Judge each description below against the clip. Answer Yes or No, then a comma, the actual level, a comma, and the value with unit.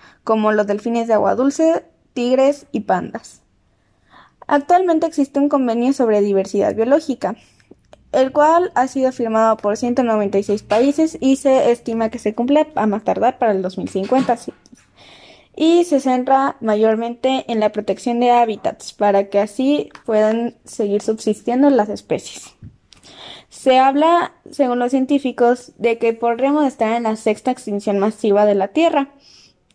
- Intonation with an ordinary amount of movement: Yes, average, 4.1 semitones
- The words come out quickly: No, average, 140 wpm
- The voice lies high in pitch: Yes, high, 240 Hz